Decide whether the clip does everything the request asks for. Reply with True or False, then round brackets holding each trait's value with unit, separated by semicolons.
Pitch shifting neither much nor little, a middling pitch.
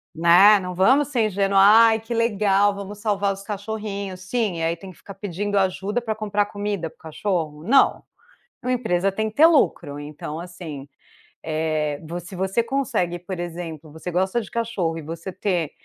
False (3.8 semitones; 195 Hz)